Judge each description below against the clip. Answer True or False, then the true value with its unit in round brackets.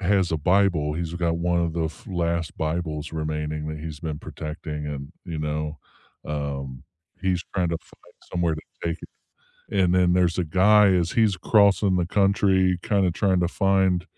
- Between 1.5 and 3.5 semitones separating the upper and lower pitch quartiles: True (3.2 semitones)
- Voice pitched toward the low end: True (85 Hz)